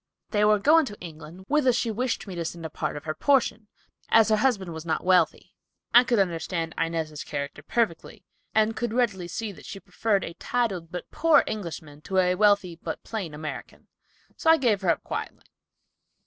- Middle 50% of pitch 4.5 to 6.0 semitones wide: Yes, average, 5.3 semitones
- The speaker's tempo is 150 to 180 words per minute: No, average, 190 wpm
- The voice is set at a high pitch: Yes, high, 195 Hz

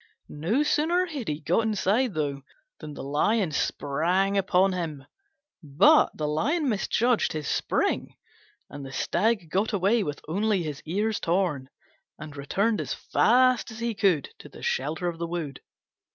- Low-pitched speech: No, medium, 185 Hz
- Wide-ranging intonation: Yes, wide, 6.5 semitones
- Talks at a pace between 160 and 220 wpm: No, average, 150 wpm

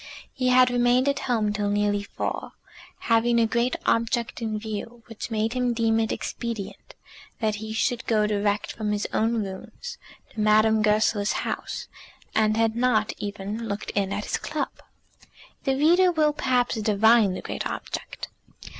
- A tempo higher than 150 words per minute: Yes, average, 160 wpm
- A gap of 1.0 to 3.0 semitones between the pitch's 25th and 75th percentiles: Yes, narrow, 2.4 semitones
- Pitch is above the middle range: Yes, high, 225 Hz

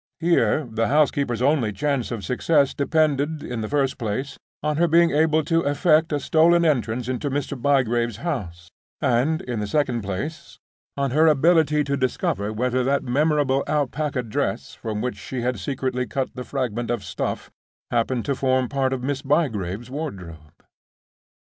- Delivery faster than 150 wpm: Yes, average, 160 wpm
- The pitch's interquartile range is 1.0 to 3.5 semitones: No, average, 4.0 semitones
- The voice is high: No, low, 135 Hz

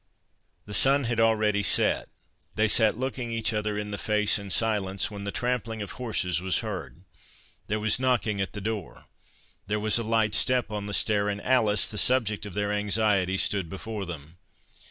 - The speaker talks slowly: No, average, 175 wpm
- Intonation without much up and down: Yes, narrow, 1.9 semitones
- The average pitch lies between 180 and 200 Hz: No, low, 105 Hz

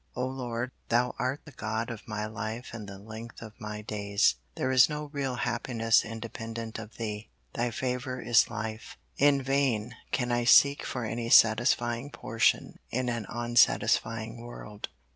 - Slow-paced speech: No, average, 160 wpm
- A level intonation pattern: Yes, narrow, 2.2 semitones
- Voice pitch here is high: No, low, 115 Hz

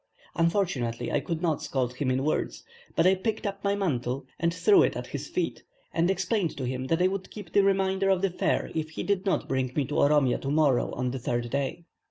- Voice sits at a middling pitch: Yes, medium, 165 Hz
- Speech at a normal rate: No, fast, 235 wpm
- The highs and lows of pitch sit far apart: Yes, wide, 6.4 semitones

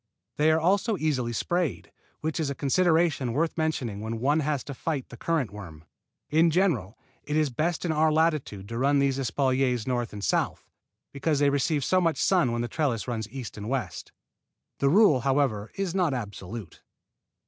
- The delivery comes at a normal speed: Yes, average, 180 wpm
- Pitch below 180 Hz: Yes, medium, 140 Hz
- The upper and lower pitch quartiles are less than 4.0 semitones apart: No, average, 5.1 semitones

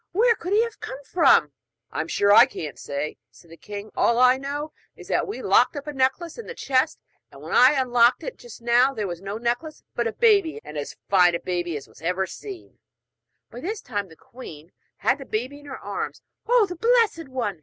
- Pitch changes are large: Yes, wide, 8.6 semitones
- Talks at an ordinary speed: No, fast, 220 wpm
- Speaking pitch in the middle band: No, very high, 255 Hz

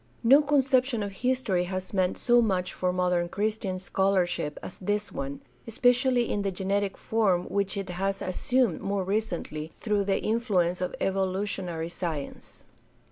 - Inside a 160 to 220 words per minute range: No, average, 150 wpm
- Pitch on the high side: Yes, high, 195 Hz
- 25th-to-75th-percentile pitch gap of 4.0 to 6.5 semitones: No, average, 3.4 semitones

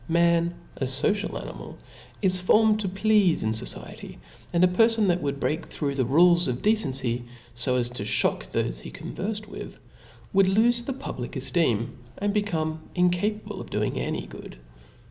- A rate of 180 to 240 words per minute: No, average, 165 wpm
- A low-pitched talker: No, medium, 175 Hz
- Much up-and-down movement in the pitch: Yes, wide, 7.5 semitones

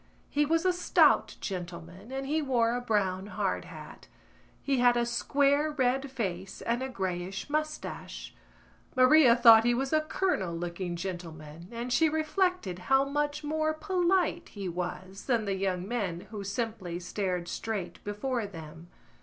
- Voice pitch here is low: No, high, 230 Hz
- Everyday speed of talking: Yes, average, 155 wpm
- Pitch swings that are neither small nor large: No, wide, 7.4 semitones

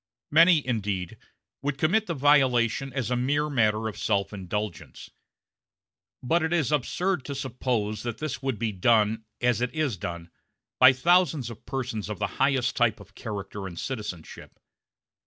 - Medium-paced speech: Yes, average, 155 wpm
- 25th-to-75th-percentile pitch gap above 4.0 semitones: Yes, average, 5.0 semitones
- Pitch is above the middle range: No, low, 120 Hz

